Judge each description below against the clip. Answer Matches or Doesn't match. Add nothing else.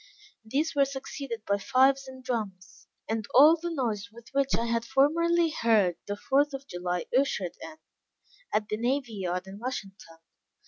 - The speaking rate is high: Doesn't match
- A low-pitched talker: Doesn't match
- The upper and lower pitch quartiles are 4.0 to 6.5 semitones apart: Matches